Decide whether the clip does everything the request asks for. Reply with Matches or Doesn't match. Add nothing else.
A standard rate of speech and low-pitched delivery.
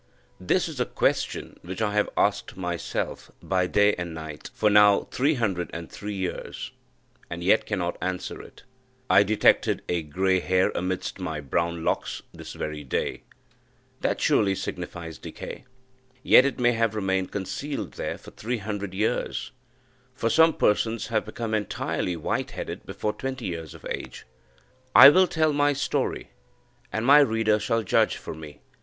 Matches